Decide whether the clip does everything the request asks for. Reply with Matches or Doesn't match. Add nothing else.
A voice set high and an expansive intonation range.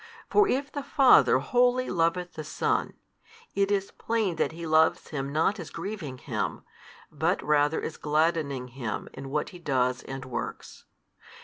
Doesn't match